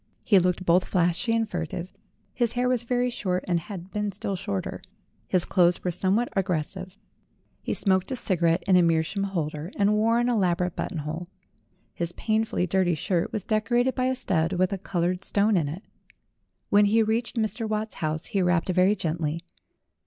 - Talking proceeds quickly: No, average, 180 wpm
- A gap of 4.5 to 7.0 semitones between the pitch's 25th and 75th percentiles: No, average, 3.8 semitones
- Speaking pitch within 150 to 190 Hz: Yes, medium, 185 Hz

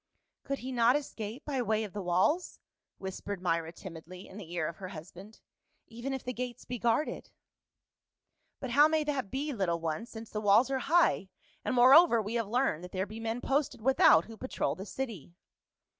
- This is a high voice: Yes, high, 225 Hz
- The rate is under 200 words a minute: No, fast, 205 wpm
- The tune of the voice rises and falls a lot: Yes, wide, 5.8 semitones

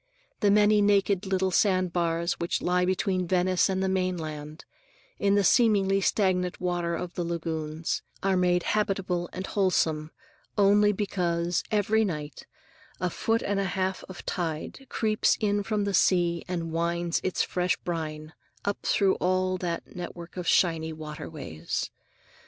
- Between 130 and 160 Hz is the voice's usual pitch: No, medium, 180 Hz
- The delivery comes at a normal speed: Yes, average, 145 wpm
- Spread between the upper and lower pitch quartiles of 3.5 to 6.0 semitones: No, narrow, 2.5 semitones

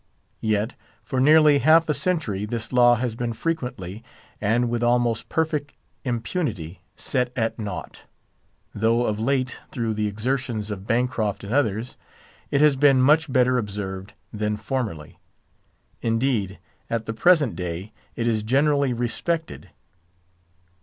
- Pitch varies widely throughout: No, average, 4.2 semitones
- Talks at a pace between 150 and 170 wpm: No, slow, 135 wpm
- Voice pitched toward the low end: Yes, low, 120 Hz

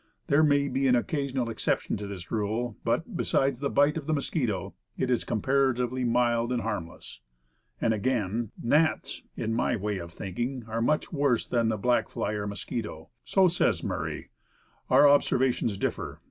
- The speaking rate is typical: Yes, average, 165 wpm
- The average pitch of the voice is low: Yes, low, 120 Hz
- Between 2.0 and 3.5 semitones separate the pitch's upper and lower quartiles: No, average, 4.4 semitones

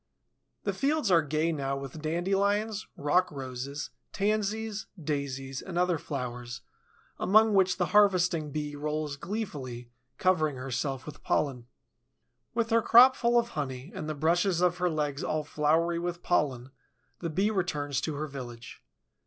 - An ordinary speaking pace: Yes, average, 145 wpm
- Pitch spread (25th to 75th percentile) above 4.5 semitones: Yes, average, 5.2 semitones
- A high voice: No, medium, 155 Hz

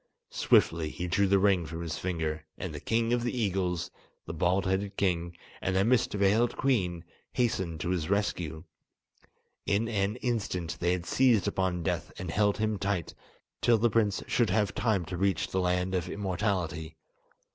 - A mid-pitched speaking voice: No, very low, 95 Hz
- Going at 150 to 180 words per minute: Yes, average, 175 wpm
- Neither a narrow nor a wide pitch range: Yes, average, 3.2 semitones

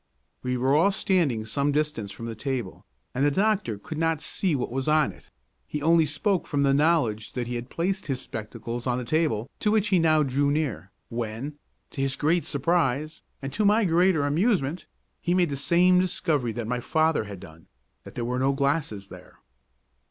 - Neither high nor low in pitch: Yes, medium, 145 Hz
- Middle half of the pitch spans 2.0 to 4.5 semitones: No, average, 5.1 semitones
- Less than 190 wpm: No, average, 195 wpm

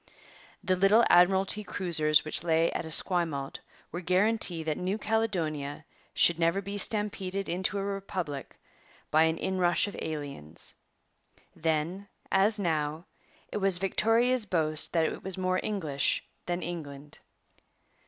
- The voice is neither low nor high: Yes, medium, 175 Hz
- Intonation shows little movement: No, average, 3.8 semitones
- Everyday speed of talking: No, slow, 130 wpm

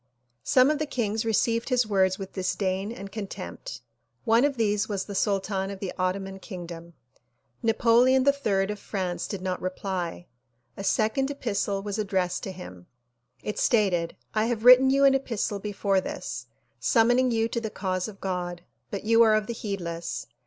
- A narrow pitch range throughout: No, average, 3.4 semitones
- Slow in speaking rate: No, average, 175 wpm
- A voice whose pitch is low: No, high, 205 Hz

